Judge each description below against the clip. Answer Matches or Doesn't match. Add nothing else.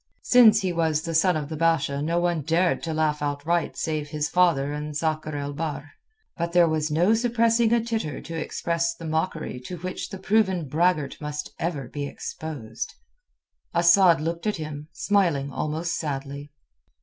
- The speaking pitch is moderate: Matches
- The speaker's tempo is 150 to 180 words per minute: Matches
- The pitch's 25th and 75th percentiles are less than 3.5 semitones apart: Matches